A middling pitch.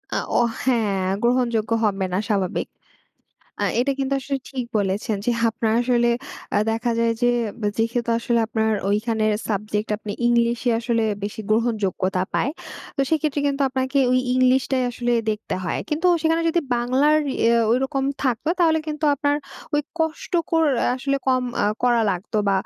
No: high, 240 Hz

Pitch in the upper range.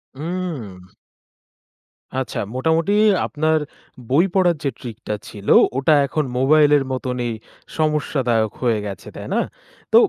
No: medium, 140 Hz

